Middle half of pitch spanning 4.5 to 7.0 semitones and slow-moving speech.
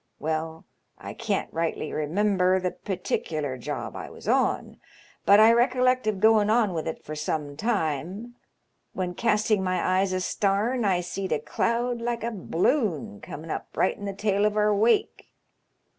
No: average, 4.9 semitones; average, 160 wpm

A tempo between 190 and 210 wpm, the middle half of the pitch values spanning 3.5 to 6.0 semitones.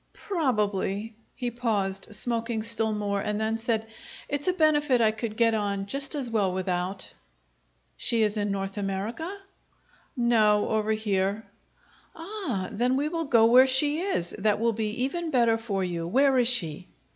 No: average, 160 wpm; average, 3.9 semitones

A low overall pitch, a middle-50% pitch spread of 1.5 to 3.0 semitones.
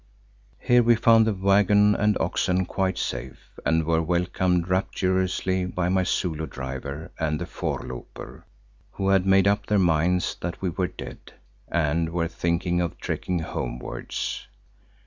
Yes: very low, 90 Hz; narrow, 2.6 semitones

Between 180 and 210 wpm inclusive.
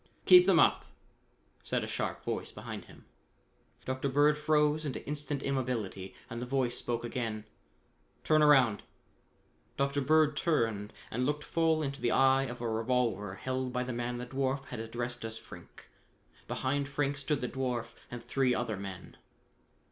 No: average, 160 wpm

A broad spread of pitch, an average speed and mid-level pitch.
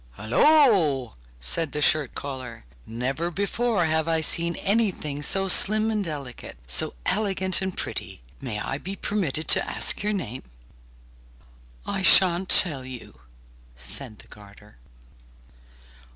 No: wide, 7.0 semitones; slow, 125 wpm; medium, 160 Hz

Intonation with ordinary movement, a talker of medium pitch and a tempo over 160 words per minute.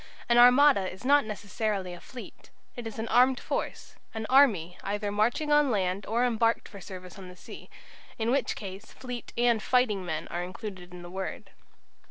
No: average, 4.6 semitones; high, 215 Hz; average, 185 wpm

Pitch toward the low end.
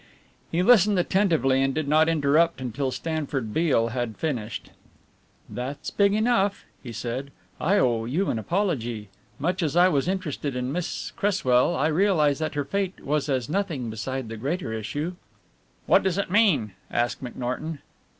No: medium, 145 Hz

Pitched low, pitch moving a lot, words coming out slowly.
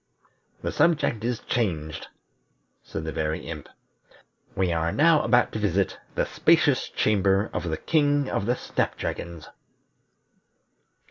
Yes: low, 100 Hz; wide, 6.8 semitones; slow, 130 wpm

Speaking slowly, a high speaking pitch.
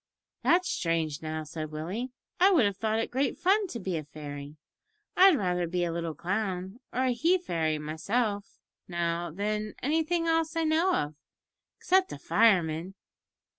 No: average, 165 wpm; high, 195 Hz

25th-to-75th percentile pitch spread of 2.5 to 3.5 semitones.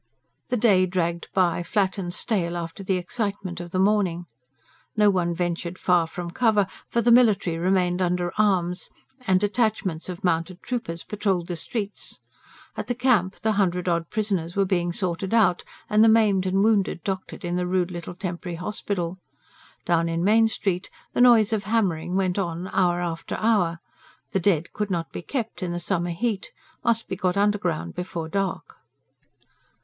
Yes: average, 3.1 semitones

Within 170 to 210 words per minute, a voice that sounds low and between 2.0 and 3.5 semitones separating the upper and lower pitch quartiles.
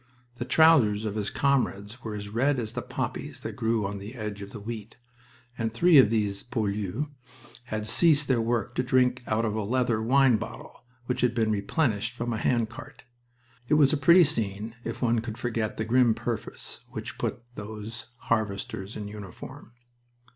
Yes: average, 185 wpm; low, 115 Hz; average, 2.9 semitones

